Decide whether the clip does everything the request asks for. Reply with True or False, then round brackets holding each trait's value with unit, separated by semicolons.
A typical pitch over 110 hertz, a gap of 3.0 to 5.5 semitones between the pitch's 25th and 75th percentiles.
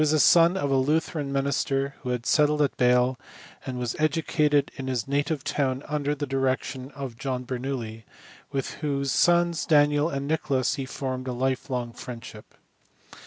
False (135 Hz; 2.4 semitones)